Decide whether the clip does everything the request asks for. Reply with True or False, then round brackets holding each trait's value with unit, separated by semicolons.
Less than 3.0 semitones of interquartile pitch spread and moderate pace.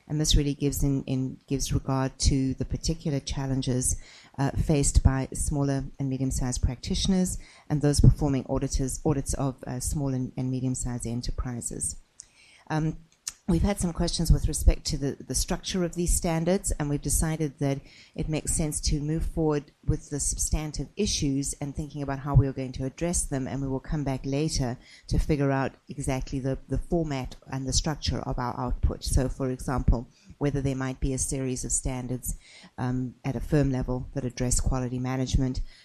True (2.4 semitones; 180 wpm)